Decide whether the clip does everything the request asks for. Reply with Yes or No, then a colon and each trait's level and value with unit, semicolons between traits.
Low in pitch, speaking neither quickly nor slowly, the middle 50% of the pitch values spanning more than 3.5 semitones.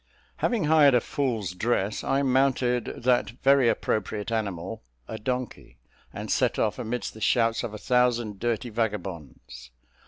No: low, 115 Hz; average, 145 wpm; average, 3.2 semitones